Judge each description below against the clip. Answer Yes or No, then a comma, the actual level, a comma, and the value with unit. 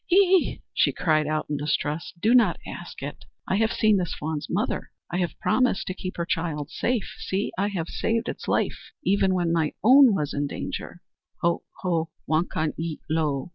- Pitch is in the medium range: Yes, medium, 175 Hz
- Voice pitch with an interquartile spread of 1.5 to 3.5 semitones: No, average, 4.7 semitones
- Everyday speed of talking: Yes, average, 195 wpm